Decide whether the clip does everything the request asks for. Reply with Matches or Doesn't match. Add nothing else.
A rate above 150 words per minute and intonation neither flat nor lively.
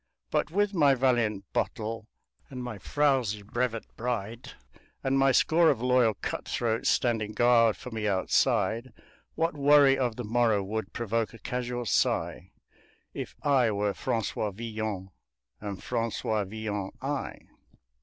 Doesn't match